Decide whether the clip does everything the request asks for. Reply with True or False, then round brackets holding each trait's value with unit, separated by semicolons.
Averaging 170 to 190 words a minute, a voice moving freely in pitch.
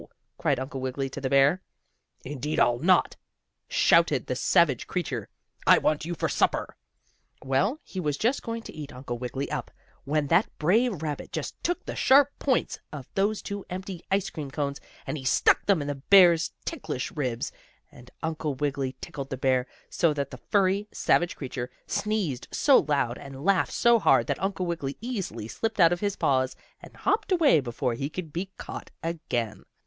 True (180 wpm; 6.4 semitones)